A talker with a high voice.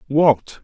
No: low, 135 Hz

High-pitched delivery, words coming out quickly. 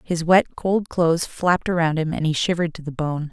No: medium, 165 Hz; fast, 235 wpm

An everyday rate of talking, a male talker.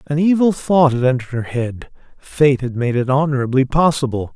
Yes: average, 180 wpm; male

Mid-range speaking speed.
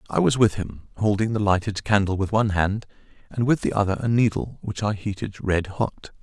No: fast, 210 wpm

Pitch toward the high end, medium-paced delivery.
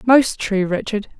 Yes: high, 215 Hz; average, 150 wpm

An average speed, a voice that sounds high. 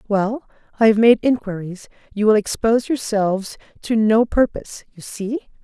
Yes: average, 150 wpm; high, 215 Hz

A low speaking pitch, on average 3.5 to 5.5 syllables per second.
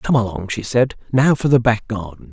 Yes: low, 115 Hz; 5.2 syllables/s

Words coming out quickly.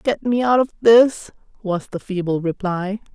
No: average, 170 wpm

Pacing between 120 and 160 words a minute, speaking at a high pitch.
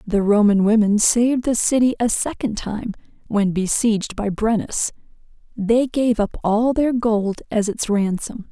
Yes: average, 155 wpm; high, 220 Hz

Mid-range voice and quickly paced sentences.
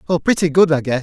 Yes: medium, 160 Hz; fast, 295 wpm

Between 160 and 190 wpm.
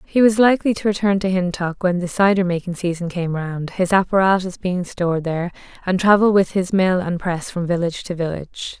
No: fast, 205 wpm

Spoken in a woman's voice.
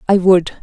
Yes: female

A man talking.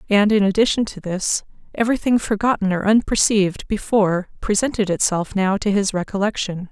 No: female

